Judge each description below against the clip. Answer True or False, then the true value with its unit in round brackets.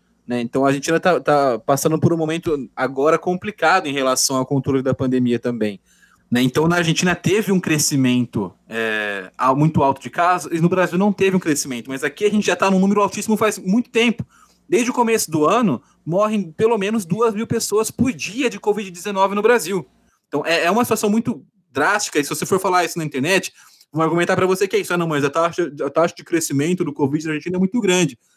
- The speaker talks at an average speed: False (215 wpm)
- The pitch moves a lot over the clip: True (6.3 semitones)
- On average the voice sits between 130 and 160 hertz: False (170 Hz)